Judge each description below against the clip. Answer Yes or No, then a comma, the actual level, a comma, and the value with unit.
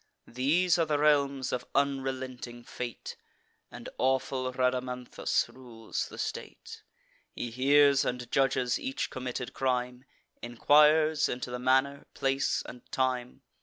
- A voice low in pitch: Yes, low, 130 Hz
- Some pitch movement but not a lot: No, narrow, 2.0 semitones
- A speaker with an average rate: No, slow, 120 wpm